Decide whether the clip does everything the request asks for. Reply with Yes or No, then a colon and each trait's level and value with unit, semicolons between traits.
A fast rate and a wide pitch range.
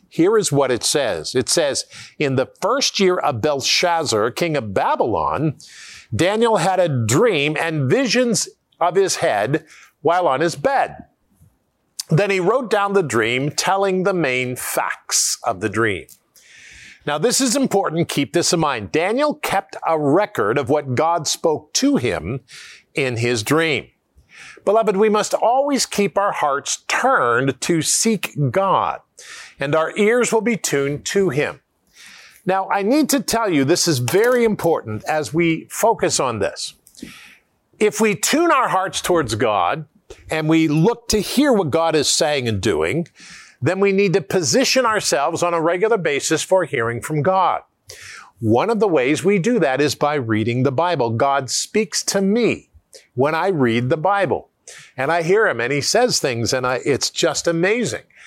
No: average, 170 wpm; wide, 7.1 semitones